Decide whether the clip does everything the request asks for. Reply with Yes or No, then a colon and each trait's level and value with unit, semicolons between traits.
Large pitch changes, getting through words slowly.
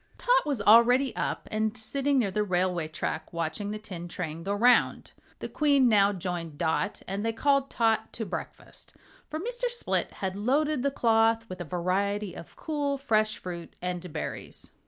No: wide, 6.4 semitones; average, 175 wpm